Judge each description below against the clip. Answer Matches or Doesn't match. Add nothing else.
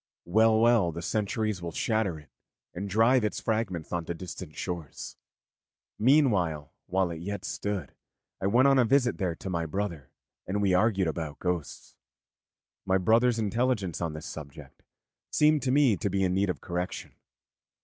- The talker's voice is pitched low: Matches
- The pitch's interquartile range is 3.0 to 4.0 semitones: Doesn't match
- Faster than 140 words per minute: Matches